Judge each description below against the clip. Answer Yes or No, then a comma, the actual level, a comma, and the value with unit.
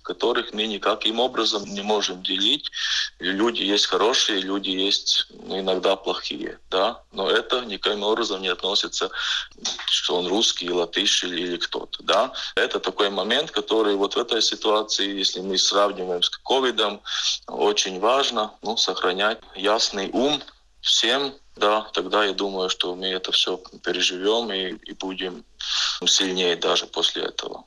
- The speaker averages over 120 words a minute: Yes, average, 140 wpm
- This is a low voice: Yes, very low, 95 Hz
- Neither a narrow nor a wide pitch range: No, narrow, 2.1 semitones